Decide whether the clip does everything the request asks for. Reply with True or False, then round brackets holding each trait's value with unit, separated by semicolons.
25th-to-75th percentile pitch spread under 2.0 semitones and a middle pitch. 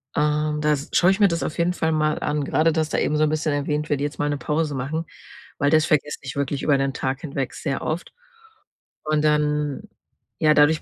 True (1.3 semitones; 150 Hz)